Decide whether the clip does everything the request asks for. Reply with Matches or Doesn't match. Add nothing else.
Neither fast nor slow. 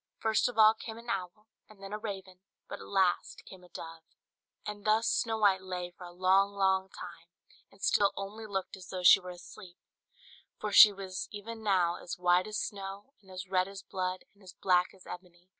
Doesn't match